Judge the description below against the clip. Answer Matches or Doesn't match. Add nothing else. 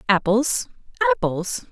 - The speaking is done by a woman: Matches